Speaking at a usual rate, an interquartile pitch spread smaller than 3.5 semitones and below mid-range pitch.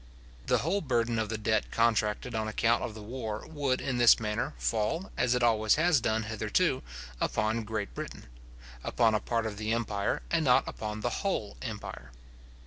Yes: average, 180 wpm; narrow, 2.4 semitones; low, 110 Hz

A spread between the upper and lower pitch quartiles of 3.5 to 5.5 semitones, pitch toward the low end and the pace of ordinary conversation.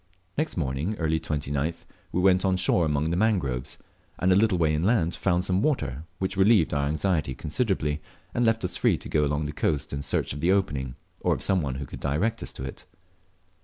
No: average, 4.8 semitones; very low, 80 Hz; fast, 210 wpm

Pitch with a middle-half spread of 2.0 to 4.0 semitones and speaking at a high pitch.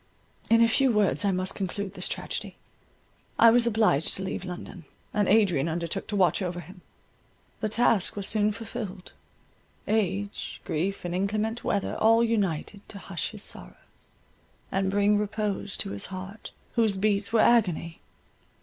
Yes: average, 2.8 semitones; high, 200 Hz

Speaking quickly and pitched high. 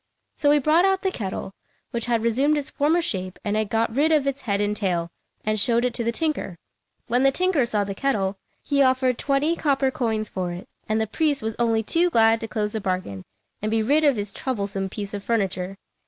Yes: fast, 225 wpm; high, 230 Hz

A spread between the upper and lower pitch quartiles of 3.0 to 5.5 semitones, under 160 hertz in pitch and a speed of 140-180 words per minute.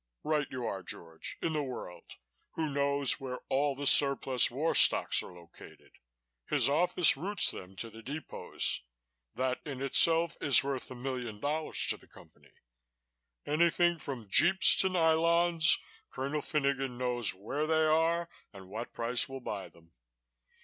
Yes: average, 4.6 semitones; medium, 140 Hz; average, 150 wpm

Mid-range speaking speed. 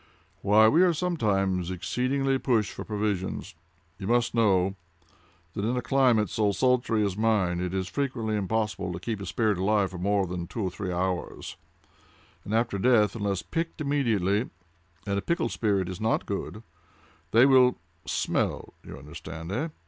Yes: average, 155 wpm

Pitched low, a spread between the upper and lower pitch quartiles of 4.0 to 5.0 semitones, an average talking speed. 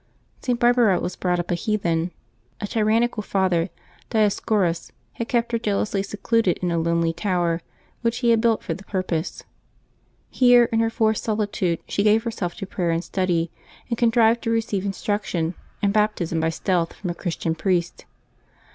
No: high, 200 Hz; average, 4.6 semitones; average, 165 wpm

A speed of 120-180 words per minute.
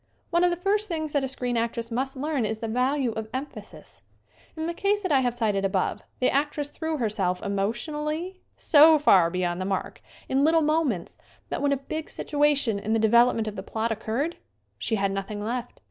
No: fast, 205 wpm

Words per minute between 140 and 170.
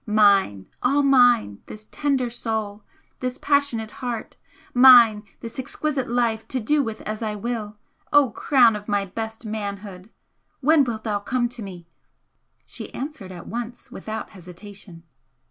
Yes: average, 145 wpm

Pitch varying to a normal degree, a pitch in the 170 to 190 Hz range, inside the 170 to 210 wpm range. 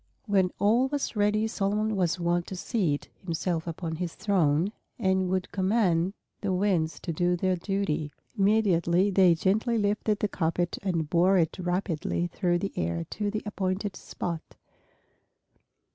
No: average, 3.1 semitones; medium, 185 Hz; average, 145 wpm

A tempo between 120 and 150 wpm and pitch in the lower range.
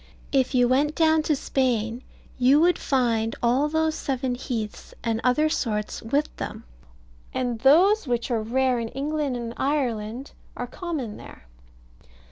No: average, 145 wpm; very high, 255 Hz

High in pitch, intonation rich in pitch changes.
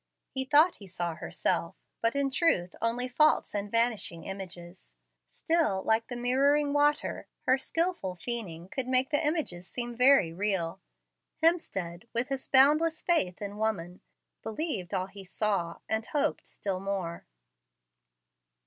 Yes: high, 225 Hz; wide, 7.1 semitones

